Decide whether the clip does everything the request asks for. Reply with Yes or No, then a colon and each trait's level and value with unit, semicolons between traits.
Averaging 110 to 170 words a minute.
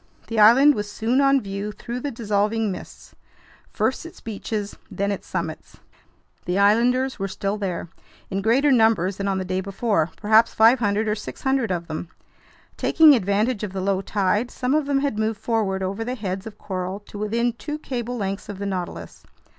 No: average, 185 wpm